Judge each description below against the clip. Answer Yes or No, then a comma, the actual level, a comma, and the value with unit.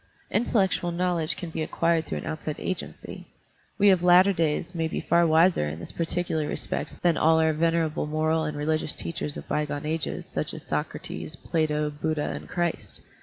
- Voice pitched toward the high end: No, medium, 160 Hz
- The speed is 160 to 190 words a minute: Yes, average, 185 wpm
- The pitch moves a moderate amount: No, narrow, 2.2 semitones